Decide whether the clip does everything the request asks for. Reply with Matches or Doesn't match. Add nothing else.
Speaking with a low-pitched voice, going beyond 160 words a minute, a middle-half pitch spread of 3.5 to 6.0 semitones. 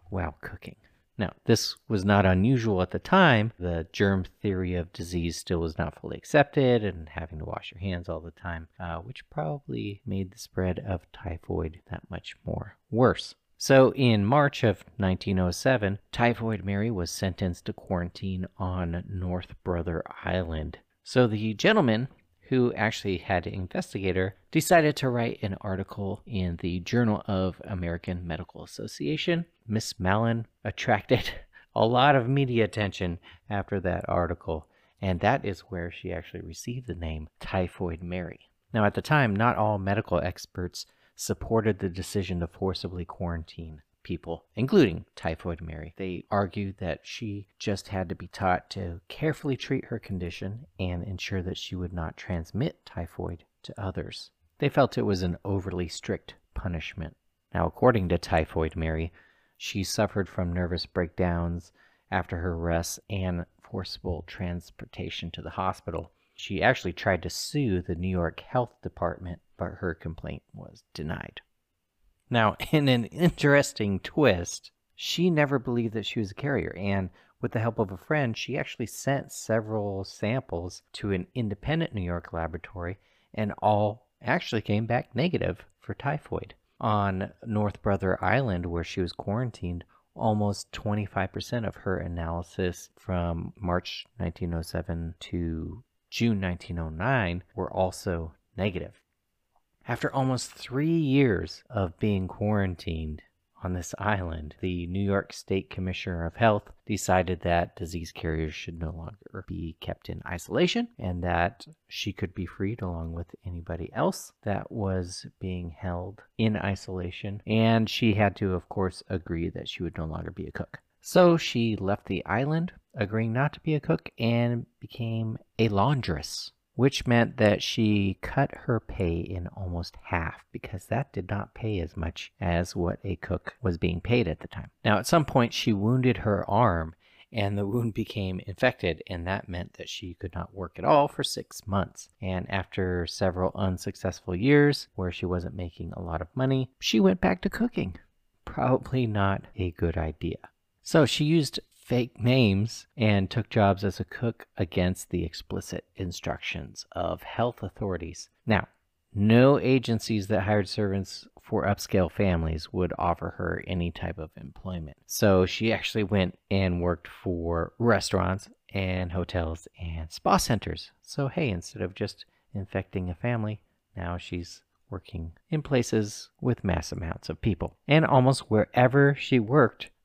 Doesn't match